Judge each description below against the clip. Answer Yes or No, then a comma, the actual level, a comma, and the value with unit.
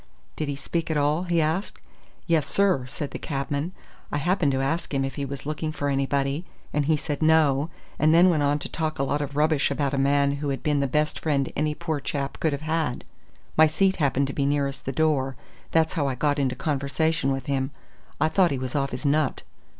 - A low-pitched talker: No, medium, 145 Hz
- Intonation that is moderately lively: No, narrow, 2.3 semitones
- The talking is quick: Yes, fast, 225 wpm